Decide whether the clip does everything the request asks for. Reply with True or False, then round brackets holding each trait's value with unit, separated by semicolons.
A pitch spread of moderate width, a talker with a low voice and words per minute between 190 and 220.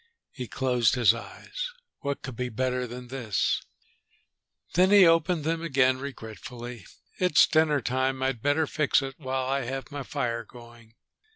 False (3.2 semitones; 130 Hz; 155 wpm)